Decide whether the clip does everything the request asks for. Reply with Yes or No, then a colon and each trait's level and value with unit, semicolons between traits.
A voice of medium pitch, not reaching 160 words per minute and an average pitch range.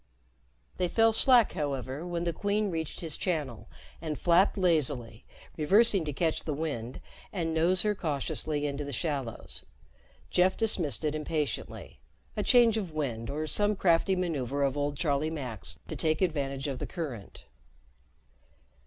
Yes: medium, 155 Hz; average, 150 wpm; average, 4.5 semitones